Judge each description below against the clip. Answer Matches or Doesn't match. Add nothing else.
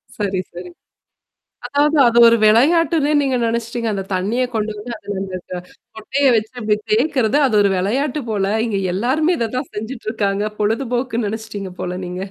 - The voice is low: Doesn't match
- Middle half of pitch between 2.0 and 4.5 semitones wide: Matches